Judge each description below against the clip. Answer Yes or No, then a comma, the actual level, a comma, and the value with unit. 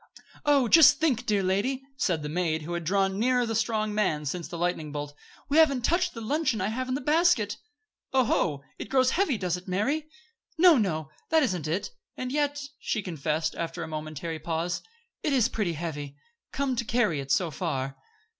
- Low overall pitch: No, high, 200 Hz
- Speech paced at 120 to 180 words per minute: No, average, 190 wpm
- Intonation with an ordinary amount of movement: No, wide, 8.0 semitones